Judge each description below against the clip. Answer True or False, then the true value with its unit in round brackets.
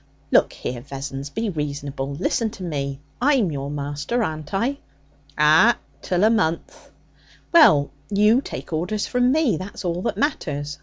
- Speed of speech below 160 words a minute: True (150 wpm)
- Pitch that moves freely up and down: True (7.5 semitones)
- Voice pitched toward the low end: False (170 Hz)